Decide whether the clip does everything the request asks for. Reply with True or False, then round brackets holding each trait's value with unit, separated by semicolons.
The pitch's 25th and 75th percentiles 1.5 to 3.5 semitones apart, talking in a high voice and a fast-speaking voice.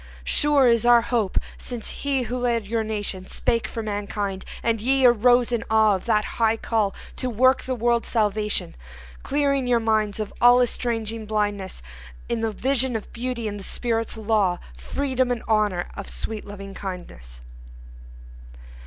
False (2.8 semitones; 225 Hz; 160 wpm)